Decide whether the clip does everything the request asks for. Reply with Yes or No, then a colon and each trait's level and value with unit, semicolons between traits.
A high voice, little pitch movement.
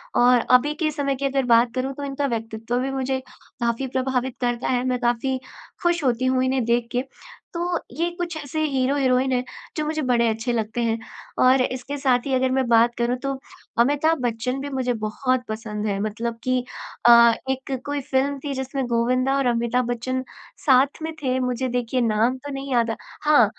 Yes: very high, 255 Hz; narrow, 2.3 semitones